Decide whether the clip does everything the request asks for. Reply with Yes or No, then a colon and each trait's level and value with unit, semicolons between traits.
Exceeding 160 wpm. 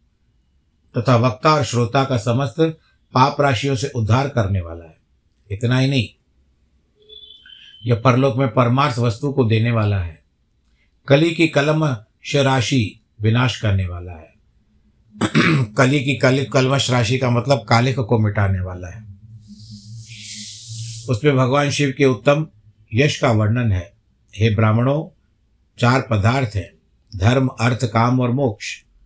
No: average, 130 wpm